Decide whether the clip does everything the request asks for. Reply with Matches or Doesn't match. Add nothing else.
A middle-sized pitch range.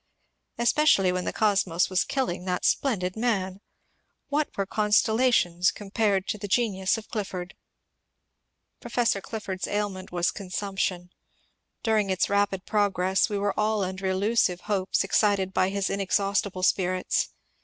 Doesn't match